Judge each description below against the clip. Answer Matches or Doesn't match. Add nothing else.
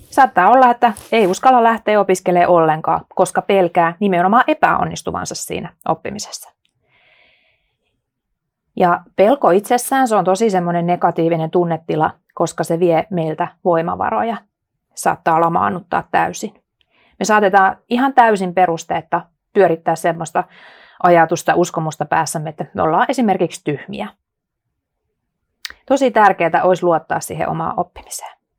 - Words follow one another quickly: Doesn't match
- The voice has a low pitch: Doesn't match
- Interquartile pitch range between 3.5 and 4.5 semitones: Matches